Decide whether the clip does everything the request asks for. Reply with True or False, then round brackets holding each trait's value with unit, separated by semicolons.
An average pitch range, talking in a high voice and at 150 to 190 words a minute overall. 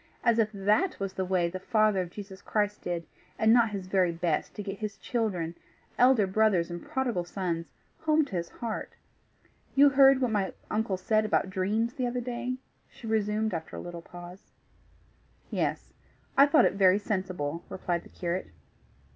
True (3.9 semitones; 200 Hz; 175 wpm)